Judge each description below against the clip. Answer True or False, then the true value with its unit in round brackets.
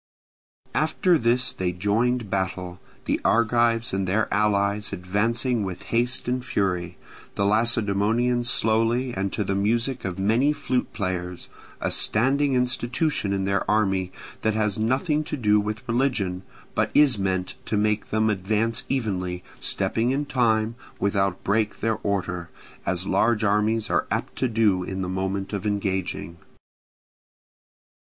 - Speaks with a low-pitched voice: True (105 Hz)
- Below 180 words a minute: True (140 wpm)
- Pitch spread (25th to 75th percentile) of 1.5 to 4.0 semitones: True (3.5 semitones)